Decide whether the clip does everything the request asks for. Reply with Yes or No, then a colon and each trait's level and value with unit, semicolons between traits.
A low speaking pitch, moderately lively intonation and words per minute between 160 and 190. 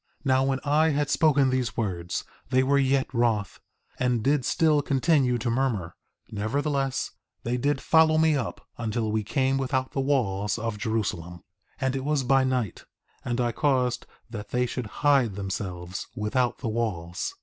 Yes: low, 125 Hz; average, 4.0 semitones; average, 170 wpm